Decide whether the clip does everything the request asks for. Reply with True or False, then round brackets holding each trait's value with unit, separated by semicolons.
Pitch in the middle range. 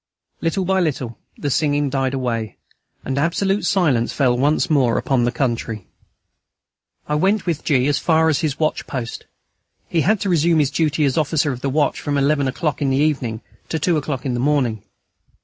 True (145 Hz)